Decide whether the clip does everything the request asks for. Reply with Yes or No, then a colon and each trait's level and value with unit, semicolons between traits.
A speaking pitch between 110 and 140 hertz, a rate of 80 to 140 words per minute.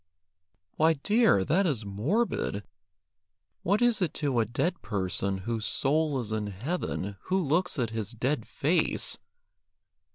Yes: low, 135 Hz; slow, 135 wpm